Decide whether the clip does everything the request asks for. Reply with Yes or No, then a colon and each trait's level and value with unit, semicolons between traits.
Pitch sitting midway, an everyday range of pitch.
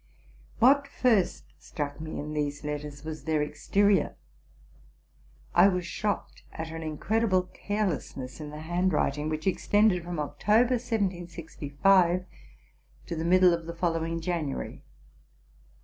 Yes: medium, 170 Hz; average, 4.2 semitones